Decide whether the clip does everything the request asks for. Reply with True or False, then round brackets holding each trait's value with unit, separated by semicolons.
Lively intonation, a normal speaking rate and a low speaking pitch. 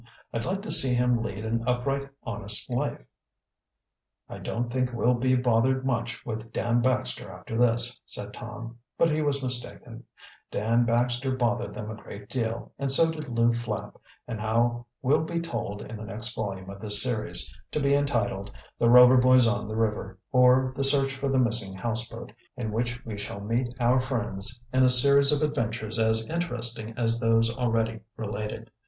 False (2.4 semitones; 180 wpm; 120 Hz)